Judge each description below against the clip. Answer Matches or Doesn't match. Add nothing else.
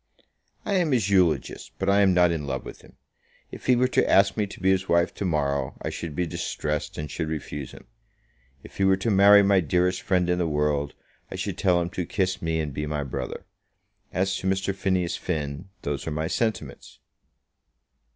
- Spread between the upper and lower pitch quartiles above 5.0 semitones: Doesn't match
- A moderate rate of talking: Doesn't match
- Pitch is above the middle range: Doesn't match